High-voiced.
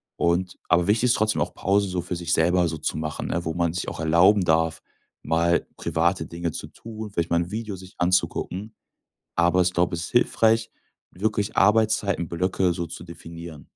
No: very low, 90 Hz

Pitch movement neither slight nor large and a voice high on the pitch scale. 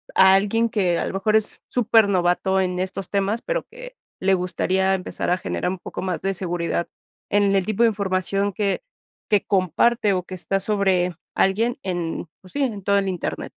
No: narrow, 2.2 semitones; high, 195 Hz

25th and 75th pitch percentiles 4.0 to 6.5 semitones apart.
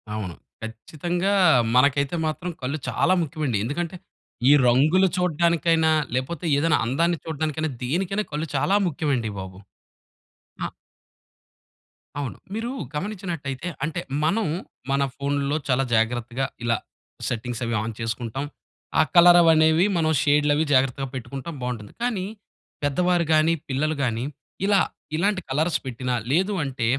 Yes: average, 4.9 semitones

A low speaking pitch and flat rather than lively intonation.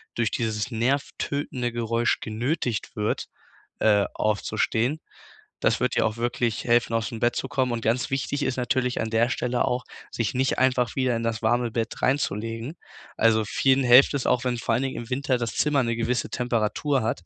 Yes: low, 120 Hz; narrow, 2.3 semitones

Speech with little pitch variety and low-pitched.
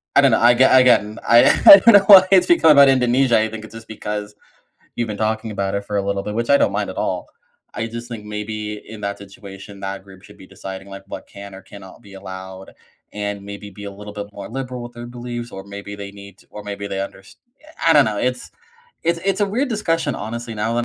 No: average, 3.3 semitones; low, 105 Hz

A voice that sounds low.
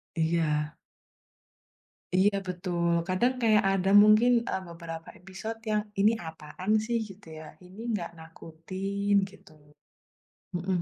No: medium, 185 Hz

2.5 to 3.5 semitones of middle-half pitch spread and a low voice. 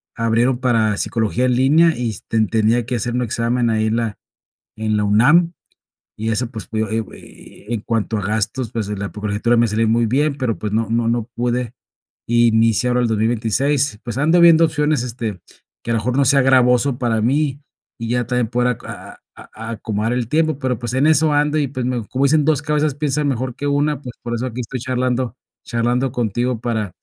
Yes: average, 2.9 semitones; low, 120 Hz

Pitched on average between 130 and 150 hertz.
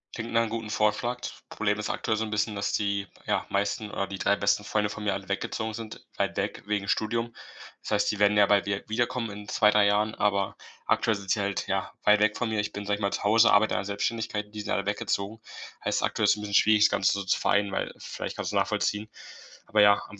No: low, 105 Hz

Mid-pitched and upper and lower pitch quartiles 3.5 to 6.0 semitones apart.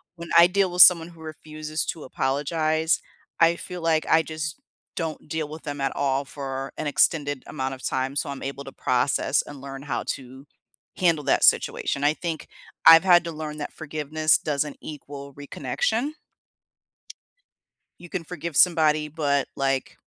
No: medium, 150 Hz; average, 2.7 semitones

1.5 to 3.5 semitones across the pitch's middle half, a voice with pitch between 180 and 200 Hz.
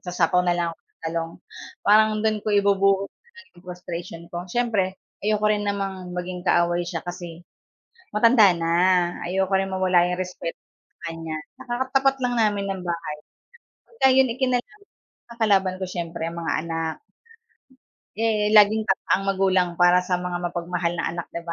Yes: average, 3.2 semitones; medium, 185 Hz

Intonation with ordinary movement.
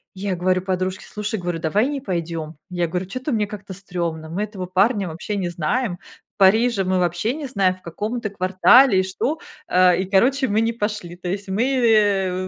Yes: average, 3.1 semitones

